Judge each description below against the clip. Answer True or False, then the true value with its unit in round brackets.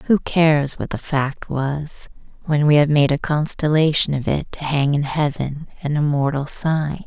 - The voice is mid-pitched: True (145 Hz)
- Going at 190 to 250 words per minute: False (180 wpm)